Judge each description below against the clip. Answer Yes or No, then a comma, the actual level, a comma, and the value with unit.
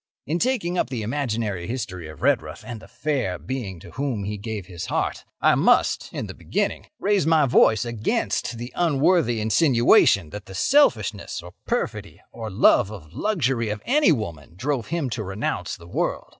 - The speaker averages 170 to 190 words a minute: Yes, average, 175 wpm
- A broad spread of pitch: Yes, wide, 6.2 semitones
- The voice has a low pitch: Yes, low, 115 Hz